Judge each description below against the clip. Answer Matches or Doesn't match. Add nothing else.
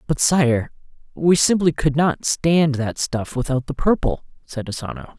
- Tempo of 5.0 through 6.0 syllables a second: Doesn't match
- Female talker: Doesn't match